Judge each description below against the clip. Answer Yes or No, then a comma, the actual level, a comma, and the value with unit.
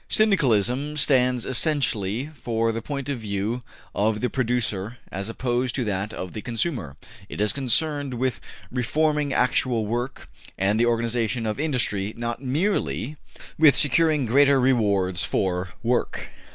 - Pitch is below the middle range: Yes, low, 120 Hz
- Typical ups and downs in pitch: Yes, average, 4.3 semitones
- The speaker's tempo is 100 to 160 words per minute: Yes, average, 140 wpm